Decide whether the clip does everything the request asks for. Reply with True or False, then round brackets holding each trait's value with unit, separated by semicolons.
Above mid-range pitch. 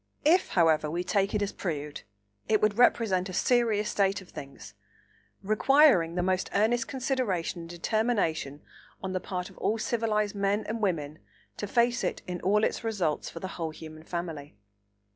True (195 Hz)